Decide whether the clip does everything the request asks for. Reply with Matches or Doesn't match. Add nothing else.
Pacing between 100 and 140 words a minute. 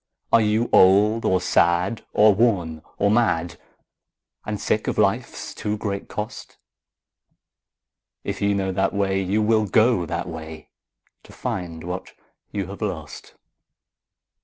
Matches